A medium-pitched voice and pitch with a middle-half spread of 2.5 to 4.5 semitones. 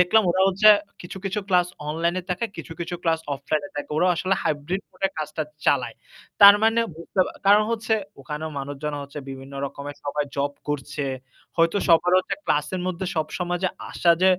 Yes: medium, 170 Hz; average, 4.1 semitones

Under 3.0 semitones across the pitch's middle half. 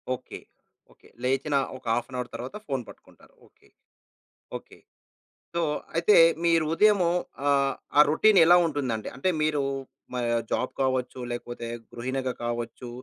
No: average, 4.4 semitones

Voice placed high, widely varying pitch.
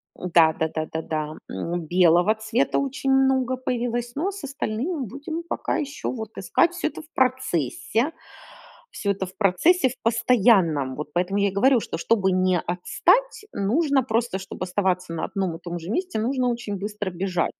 Yes: high, 215 Hz; wide, 6.5 semitones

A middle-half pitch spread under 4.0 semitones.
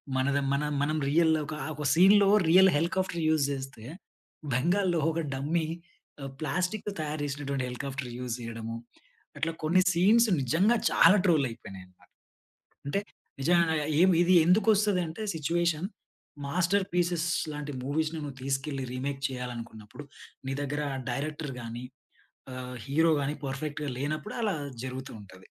No: average, 4.3 semitones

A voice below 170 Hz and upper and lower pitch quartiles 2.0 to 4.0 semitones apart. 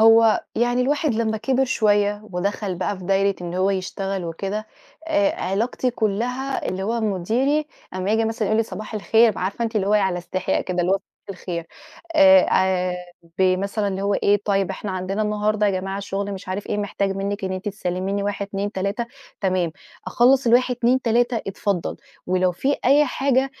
No: high, 205 Hz; average, 3.3 semitones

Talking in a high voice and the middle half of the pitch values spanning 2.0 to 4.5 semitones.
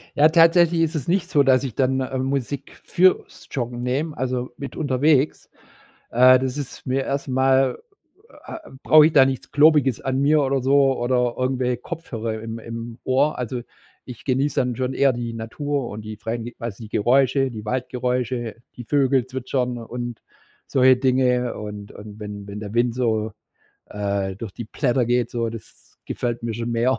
No: low, 125 Hz; narrow, 2.6 semitones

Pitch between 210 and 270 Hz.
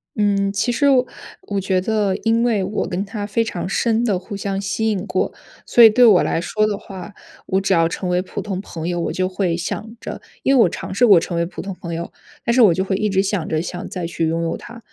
No: high, 195 Hz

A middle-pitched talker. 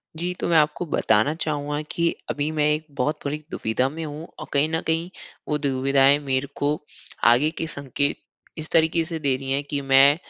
Yes: medium, 145 Hz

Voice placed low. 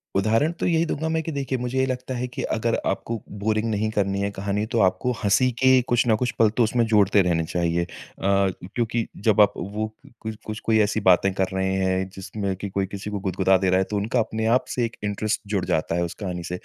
Yes: low, 105 Hz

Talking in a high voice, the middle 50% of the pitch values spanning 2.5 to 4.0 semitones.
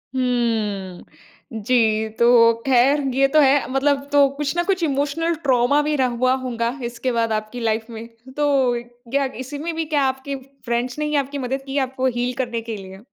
Yes: very high, 260 Hz; average, 3.3 semitones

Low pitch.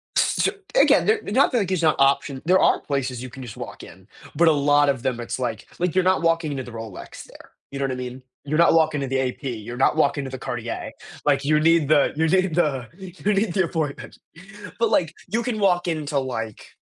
No: medium, 145 Hz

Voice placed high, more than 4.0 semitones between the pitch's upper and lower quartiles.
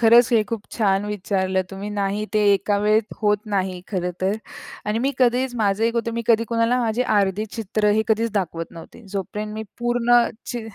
No: high, 215 Hz; average, 2.9 semitones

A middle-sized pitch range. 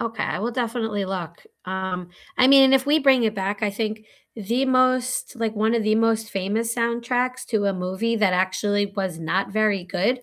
Yes: average, 3.7 semitones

